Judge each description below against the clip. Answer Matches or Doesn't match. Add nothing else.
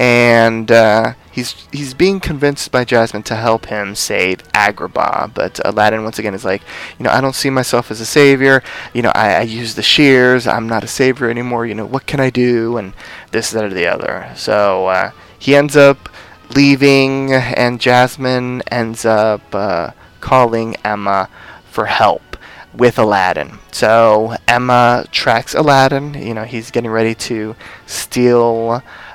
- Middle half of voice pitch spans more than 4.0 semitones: Doesn't match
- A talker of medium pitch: Doesn't match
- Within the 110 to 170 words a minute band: Matches